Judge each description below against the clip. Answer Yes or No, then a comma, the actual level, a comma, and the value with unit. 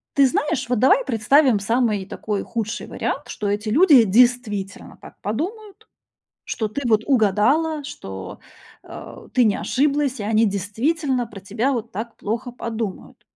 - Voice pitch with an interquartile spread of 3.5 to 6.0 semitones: Yes, average, 4.8 semitones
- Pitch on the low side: No, high, 235 Hz